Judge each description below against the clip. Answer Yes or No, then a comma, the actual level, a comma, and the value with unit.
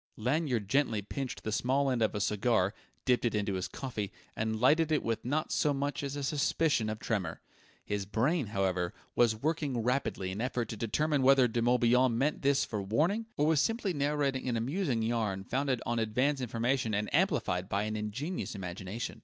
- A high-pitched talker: No, low, 120 Hz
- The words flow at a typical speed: Yes, average, 185 wpm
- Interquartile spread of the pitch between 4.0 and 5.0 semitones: Yes, average, 4.7 semitones